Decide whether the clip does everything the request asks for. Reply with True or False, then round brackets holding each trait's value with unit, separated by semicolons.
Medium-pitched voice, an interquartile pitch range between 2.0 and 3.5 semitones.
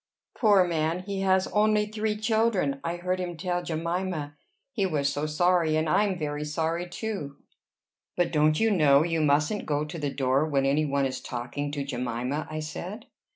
False (160 Hz; 4.4 semitones)